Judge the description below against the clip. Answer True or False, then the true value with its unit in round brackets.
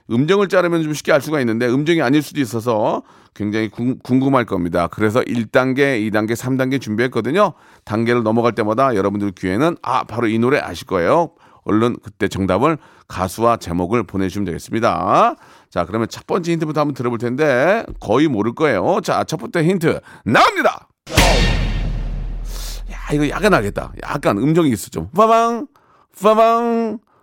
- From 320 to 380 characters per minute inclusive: True (340 characters per minute)